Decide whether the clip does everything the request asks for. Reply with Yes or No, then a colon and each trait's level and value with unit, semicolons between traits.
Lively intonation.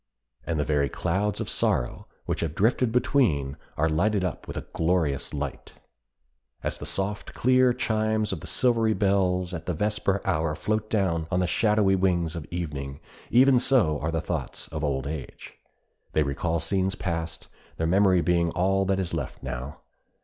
No: average, 4.9 semitones